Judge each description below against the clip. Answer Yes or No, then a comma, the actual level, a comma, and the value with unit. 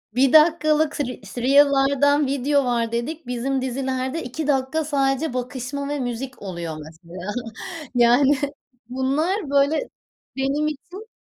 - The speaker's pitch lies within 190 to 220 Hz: No, very high, 270 Hz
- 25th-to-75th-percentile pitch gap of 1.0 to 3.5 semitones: Yes, average, 2.8 semitones